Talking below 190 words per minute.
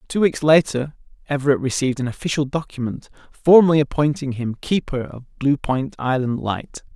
Yes: average, 145 wpm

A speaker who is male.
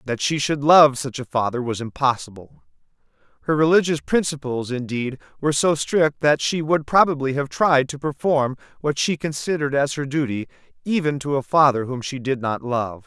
Yes: male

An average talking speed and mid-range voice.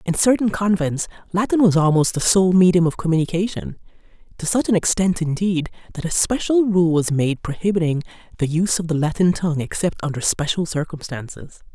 Yes: average, 165 wpm; medium, 170 Hz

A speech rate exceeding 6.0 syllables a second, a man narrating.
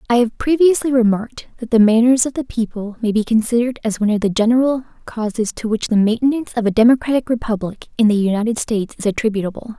No: 6.8 syllables/s; female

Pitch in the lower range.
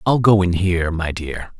Yes: very low, 95 Hz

